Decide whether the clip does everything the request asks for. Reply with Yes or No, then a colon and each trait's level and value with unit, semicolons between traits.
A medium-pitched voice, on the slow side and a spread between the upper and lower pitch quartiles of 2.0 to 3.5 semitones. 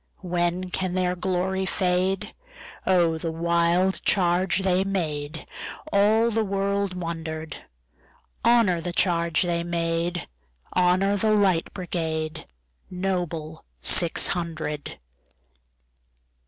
Yes: medium, 175 Hz; slow, 80 wpm; narrow, 2.5 semitones